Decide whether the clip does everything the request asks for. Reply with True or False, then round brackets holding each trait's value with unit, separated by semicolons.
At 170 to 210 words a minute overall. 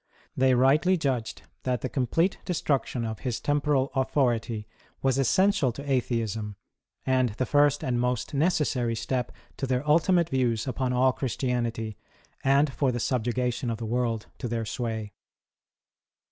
False (145 wpm)